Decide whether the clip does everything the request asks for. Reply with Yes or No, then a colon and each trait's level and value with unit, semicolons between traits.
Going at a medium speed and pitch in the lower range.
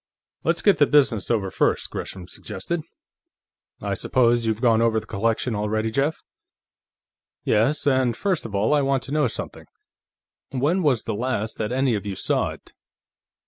Yes: average, 165 wpm; low, 120 Hz